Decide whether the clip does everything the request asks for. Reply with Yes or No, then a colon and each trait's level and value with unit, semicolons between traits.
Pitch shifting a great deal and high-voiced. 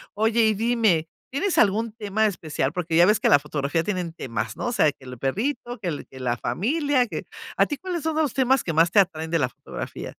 Yes: wide, 7.4 semitones; high, 200 Hz